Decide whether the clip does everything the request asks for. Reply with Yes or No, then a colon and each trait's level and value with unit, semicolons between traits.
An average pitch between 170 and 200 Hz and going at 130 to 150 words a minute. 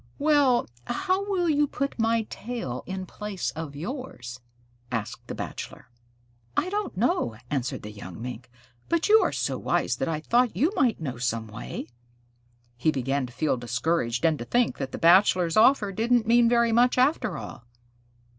No: high, 190 Hz; average, 170 wpm